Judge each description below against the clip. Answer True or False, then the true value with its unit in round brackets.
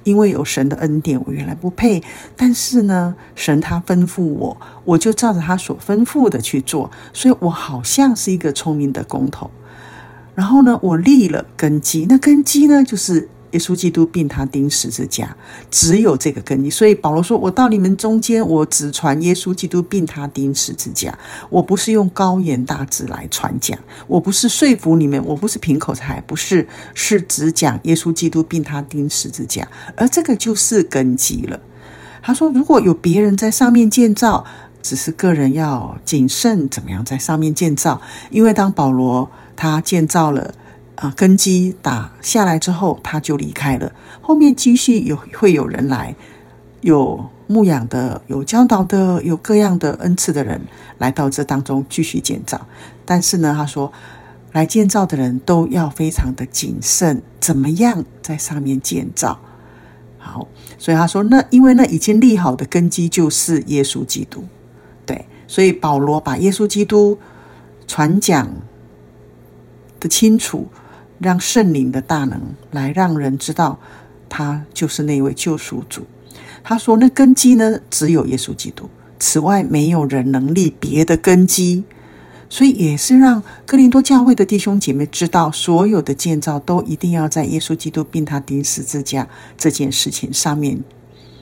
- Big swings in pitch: True (6.3 semitones)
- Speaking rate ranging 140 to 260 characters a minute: True (245 characters per minute)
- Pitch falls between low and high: True (160 Hz)